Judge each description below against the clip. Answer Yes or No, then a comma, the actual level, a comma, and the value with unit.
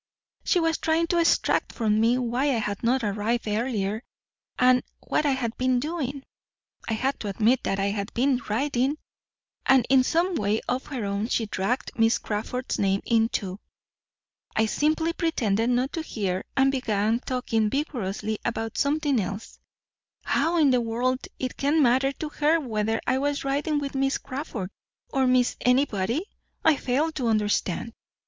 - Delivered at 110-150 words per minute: No, average, 165 wpm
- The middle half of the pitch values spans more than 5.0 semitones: No, average, 4.2 semitones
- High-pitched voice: Yes, very high, 250 Hz